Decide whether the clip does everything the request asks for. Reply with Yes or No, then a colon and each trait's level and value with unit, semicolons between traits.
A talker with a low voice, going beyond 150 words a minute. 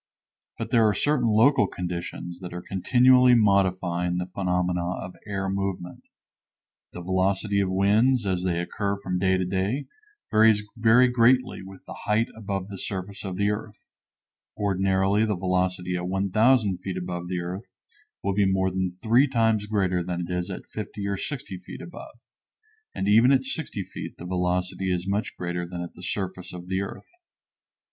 Yes: very low, 95 Hz; average, 170 wpm